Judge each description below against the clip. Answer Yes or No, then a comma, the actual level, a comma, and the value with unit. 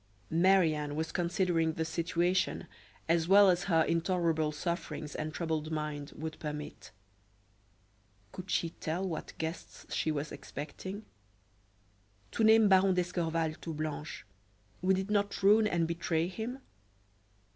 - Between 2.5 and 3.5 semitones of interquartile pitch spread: Yes, average, 3.0 semitones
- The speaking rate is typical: No, slow, 130 wpm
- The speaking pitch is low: No, medium, 170 Hz